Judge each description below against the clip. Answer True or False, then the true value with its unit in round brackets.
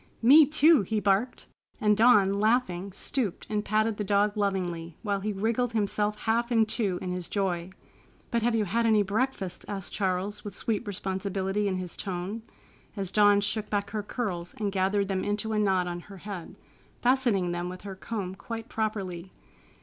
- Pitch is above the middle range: True (205 Hz)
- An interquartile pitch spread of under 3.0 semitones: True (2.5 semitones)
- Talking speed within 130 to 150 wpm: False (180 wpm)